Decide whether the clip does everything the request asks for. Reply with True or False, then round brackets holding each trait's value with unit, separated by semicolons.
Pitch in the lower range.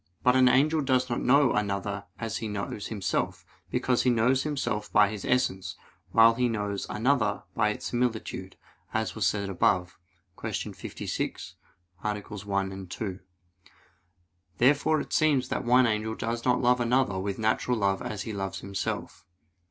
True (110 Hz)